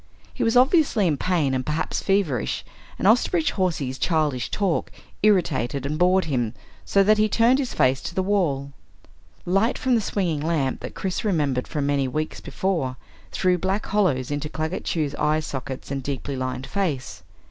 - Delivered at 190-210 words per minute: No, average, 170 wpm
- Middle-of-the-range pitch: Yes, medium, 160 Hz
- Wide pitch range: Yes, wide, 6.2 semitones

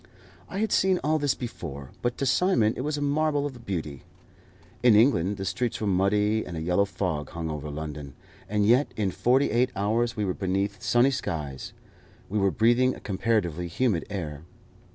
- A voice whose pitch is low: Yes, low, 105 Hz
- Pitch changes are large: Yes, wide, 6.3 semitones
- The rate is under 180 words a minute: No, average, 185 wpm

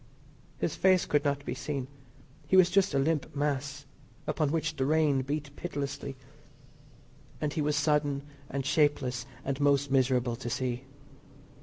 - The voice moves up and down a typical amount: No, narrow, 2.0 semitones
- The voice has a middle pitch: Yes, medium, 145 Hz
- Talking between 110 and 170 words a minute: Yes, average, 150 wpm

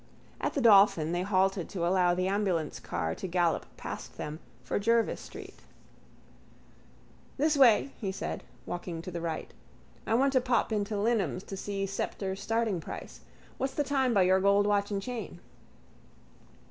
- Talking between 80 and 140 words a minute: No, average, 160 wpm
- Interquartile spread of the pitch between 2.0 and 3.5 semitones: No, average, 3.9 semitones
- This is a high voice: Yes, high, 195 Hz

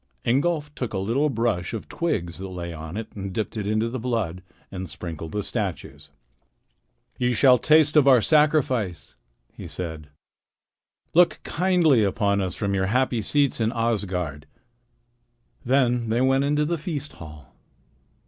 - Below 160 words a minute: Yes, average, 150 wpm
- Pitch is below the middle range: Yes, low, 115 Hz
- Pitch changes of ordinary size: No, wide, 6.5 semitones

